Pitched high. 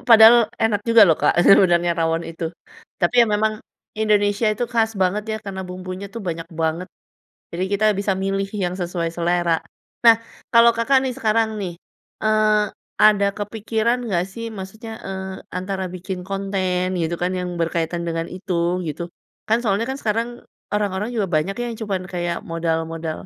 Yes: high, 195 Hz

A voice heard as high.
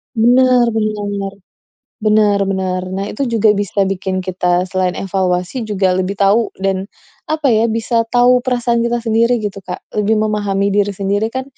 Yes: high, 205 Hz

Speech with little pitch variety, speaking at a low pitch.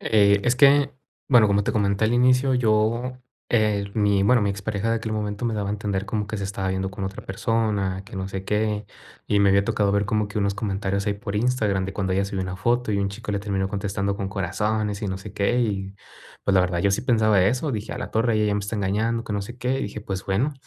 Yes: narrow, 2.2 semitones; low, 105 Hz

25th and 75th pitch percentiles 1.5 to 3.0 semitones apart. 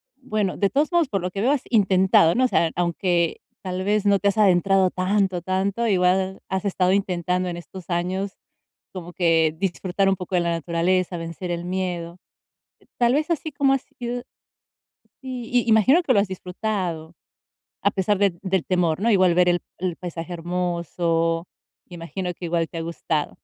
Yes: average, 2.7 semitones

